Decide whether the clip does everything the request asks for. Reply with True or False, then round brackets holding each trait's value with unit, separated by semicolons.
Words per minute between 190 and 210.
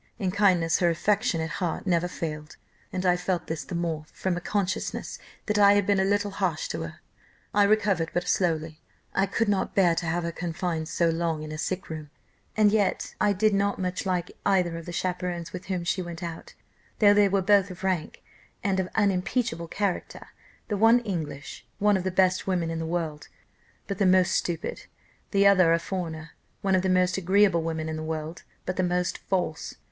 True (205 wpm)